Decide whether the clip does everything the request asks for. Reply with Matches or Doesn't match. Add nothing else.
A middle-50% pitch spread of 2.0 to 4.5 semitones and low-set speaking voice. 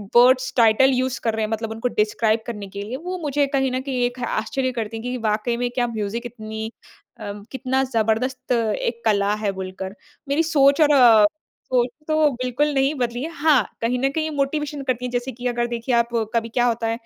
Doesn't match